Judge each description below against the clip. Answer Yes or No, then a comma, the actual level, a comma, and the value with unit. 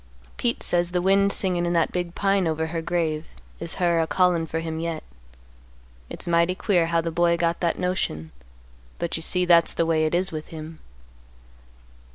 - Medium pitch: Yes, medium, 170 Hz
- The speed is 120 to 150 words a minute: No, average, 190 wpm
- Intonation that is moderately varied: No, narrow, 1.6 semitones